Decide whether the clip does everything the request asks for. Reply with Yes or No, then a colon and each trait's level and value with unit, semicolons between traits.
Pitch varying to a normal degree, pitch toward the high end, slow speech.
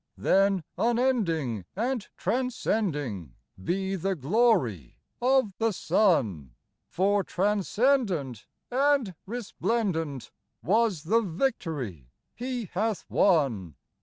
No: wide, 7.7 semitones; high, 195 Hz; slow, 90 wpm